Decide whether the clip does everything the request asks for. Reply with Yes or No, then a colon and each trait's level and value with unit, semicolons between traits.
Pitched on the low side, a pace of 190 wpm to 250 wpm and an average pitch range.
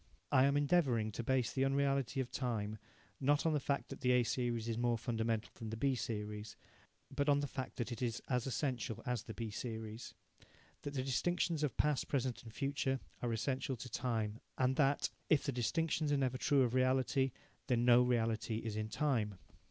Yes: low, 125 Hz; average, 200 wpm; average, 3.3 semitones